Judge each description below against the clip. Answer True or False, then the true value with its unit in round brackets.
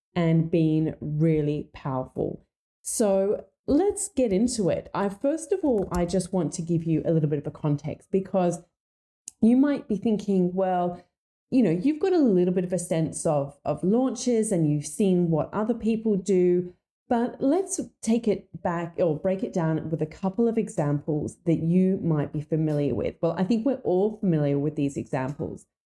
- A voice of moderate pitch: True (180 Hz)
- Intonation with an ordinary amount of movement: False (5.8 semitones)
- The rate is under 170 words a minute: False (185 wpm)